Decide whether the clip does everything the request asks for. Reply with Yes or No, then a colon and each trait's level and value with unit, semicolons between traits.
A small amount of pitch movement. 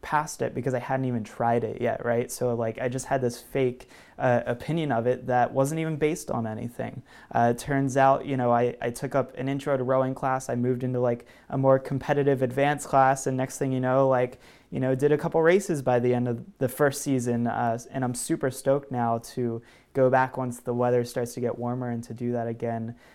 Yes: narrow, 2.0 semitones